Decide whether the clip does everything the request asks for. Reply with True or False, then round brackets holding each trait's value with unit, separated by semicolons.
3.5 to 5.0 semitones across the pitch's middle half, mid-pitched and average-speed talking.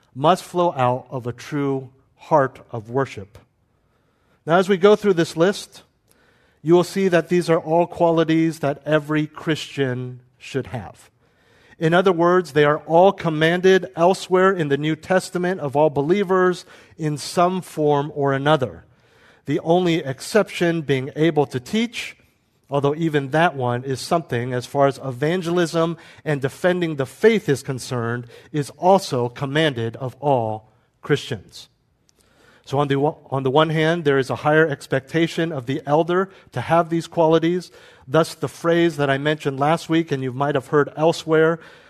True (4.0 semitones; 150 Hz; 160 wpm)